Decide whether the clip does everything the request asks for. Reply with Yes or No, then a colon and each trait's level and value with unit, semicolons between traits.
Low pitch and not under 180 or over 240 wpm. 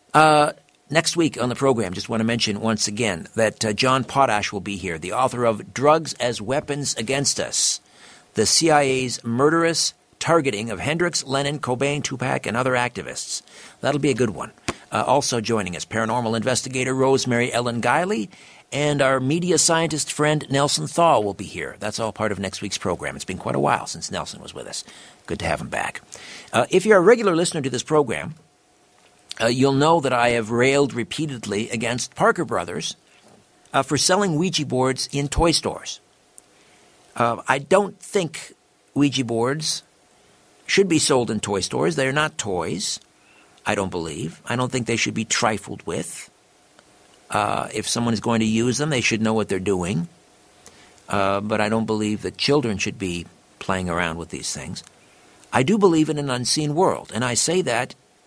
Yes: low, 130 Hz; average, 185 wpm